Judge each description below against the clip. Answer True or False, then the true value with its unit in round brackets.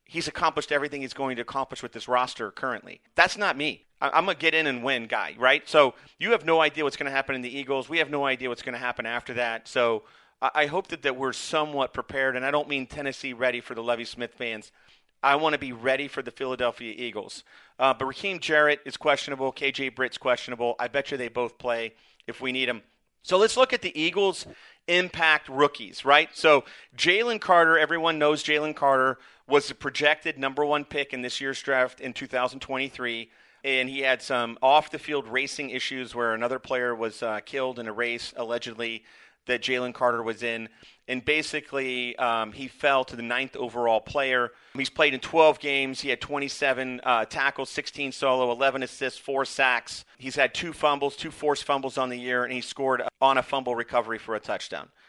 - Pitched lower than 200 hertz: True (135 Hz)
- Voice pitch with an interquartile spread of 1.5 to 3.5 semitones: True (3.0 semitones)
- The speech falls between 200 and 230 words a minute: True (205 wpm)